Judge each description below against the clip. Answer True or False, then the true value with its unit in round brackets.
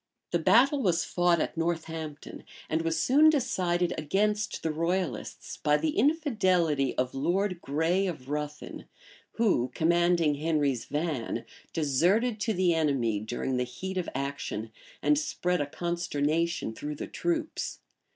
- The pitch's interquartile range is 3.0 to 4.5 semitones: True (4.1 semitones)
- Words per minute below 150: True (135 wpm)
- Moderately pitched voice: True (165 Hz)